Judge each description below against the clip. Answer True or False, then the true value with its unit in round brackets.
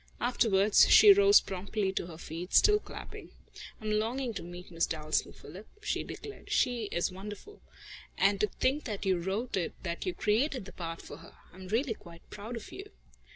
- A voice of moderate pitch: False (205 Hz)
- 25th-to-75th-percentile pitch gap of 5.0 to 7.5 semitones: True (5.3 semitones)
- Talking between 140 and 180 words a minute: False (190 wpm)